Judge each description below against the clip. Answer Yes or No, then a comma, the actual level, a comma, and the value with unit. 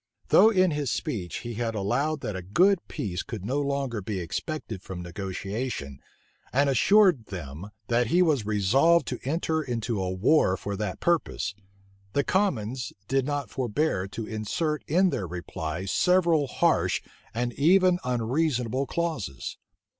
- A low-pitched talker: Yes, low, 125 Hz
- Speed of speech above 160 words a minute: No, average, 145 wpm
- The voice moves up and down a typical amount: No, wide, 7.5 semitones